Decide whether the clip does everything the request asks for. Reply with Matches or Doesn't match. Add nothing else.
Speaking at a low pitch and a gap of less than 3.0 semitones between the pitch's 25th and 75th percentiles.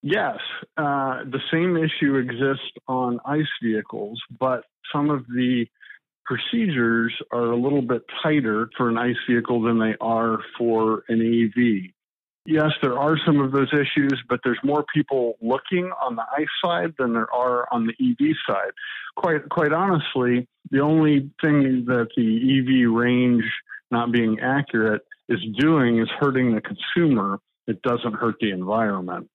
Doesn't match